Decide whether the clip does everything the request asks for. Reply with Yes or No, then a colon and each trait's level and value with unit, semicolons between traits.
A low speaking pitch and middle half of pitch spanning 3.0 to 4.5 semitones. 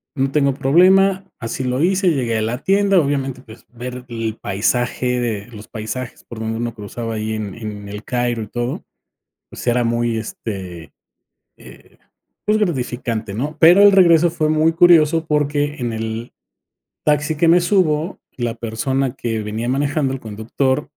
No: low, 125 Hz; average, 5.3 semitones